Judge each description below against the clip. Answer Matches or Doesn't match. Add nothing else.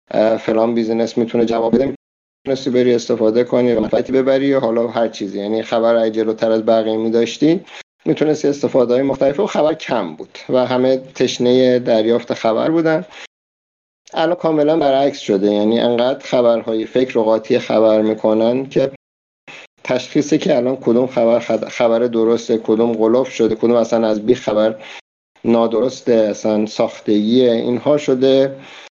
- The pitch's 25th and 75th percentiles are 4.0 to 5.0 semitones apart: Doesn't match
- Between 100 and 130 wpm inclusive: Doesn't match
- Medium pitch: Doesn't match